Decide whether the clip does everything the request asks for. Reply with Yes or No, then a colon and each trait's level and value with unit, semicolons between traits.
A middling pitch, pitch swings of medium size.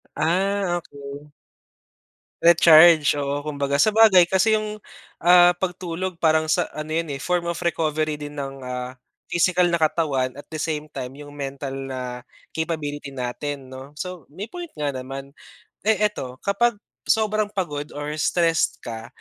Yes: medium, 155 Hz; average, 4.1 semitones